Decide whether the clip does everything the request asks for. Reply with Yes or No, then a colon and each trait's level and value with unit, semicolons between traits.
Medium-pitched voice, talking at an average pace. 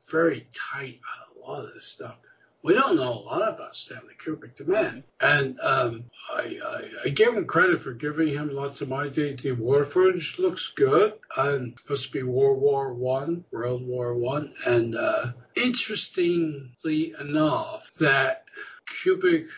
Yes: medium, 150 Hz; average, 160 wpm